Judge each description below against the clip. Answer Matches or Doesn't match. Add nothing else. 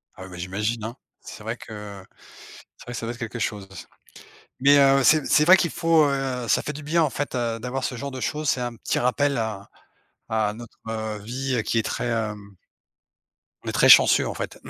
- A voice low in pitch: Matches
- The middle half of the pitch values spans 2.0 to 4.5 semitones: Matches